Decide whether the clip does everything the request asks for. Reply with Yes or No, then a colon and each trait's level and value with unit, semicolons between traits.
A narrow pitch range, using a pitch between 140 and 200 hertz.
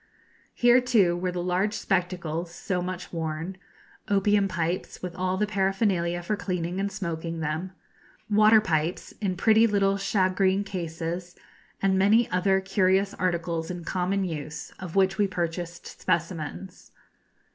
Yes: narrow, 2.3 semitones; medium, 185 Hz